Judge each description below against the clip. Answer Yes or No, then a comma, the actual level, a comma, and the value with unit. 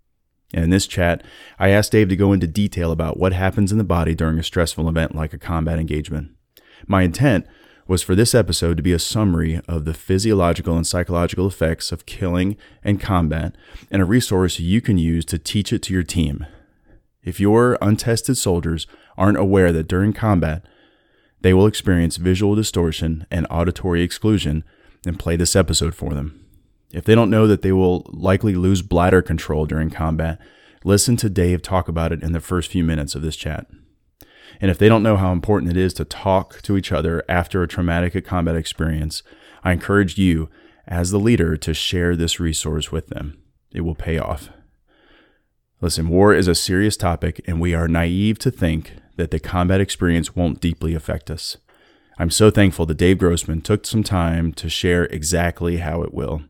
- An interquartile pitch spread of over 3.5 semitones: No, average, 2.9 semitones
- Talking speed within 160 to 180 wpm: No, average, 190 wpm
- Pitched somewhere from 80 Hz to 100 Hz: Yes, very low, 85 Hz